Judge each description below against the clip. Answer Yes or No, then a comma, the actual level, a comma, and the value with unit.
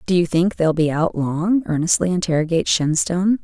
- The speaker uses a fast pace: No, average, 175 wpm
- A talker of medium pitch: Yes, medium, 170 Hz